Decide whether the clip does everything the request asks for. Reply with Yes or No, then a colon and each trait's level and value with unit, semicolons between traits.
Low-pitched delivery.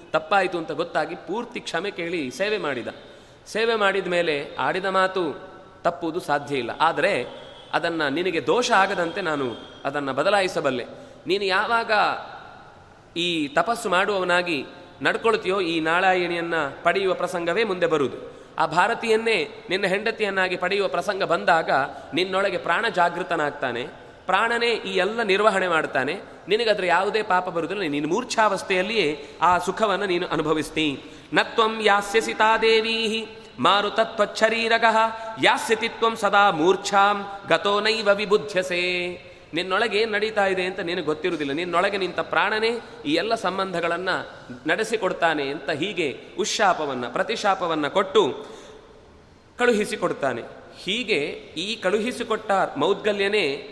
No: high, 195 Hz